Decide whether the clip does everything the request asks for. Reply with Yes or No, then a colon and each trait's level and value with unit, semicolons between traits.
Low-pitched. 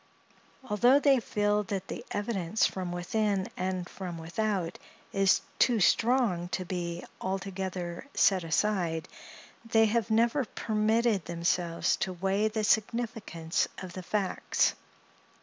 No: high, 195 Hz